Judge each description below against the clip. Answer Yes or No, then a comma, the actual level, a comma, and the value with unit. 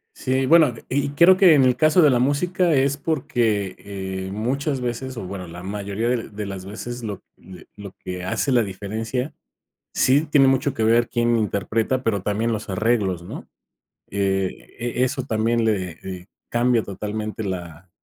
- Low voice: Yes, low, 115 Hz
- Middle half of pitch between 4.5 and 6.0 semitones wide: Yes, average, 4.8 semitones